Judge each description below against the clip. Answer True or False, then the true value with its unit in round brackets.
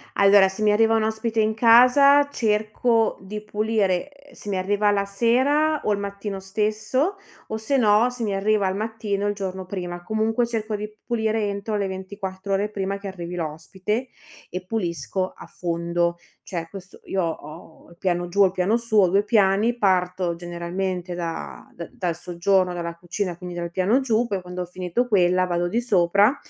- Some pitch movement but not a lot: True (3.4 semitones)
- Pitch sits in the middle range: False (200 Hz)